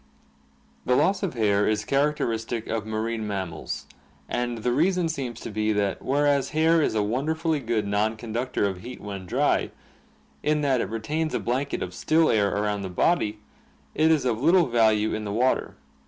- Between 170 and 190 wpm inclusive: Yes, average, 180 wpm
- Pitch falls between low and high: No, low, 115 Hz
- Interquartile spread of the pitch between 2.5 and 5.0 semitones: No, wide, 5.5 semitones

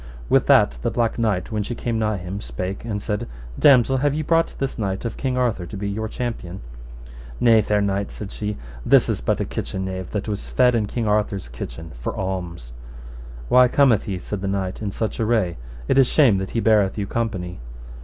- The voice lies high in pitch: No, low, 105 Hz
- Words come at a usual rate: No, fast, 210 wpm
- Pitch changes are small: No, average, 3.5 semitones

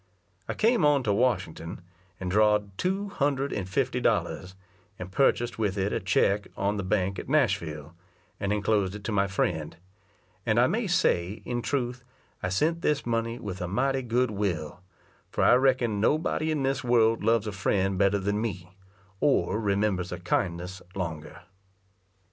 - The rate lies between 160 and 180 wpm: Yes, average, 165 wpm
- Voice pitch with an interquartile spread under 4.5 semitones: No, average, 4.8 semitones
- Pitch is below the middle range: Yes, low, 105 Hz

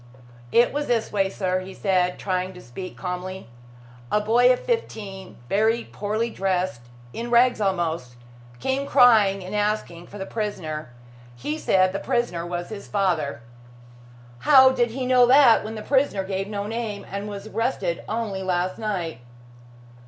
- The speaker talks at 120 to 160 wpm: Yes, average, 155 wpm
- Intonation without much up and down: No, average, 3.9 semitones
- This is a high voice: Yes, high, 200 Hz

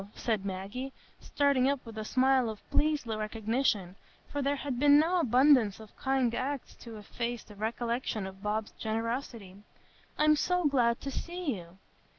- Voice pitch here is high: Yes, high, 240 Hz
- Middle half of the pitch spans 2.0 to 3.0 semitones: No, average, 4.4 semitones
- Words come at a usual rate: Yes, average, 160 wpm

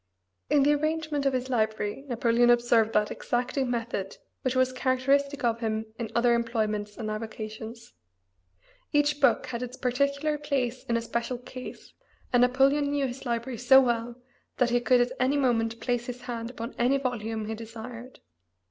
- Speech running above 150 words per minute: Yes, average, 165 wpm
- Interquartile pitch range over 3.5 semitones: No, narrow, 2.5 semitones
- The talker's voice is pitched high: Yes, high, 245 Hz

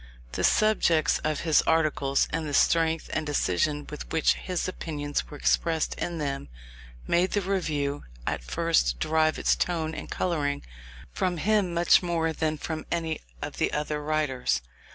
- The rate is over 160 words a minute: No, average, 155 wpm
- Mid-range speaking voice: Yes, medium, 155 Hz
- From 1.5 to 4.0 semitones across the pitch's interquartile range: Yes, narrow, 2.5 semitones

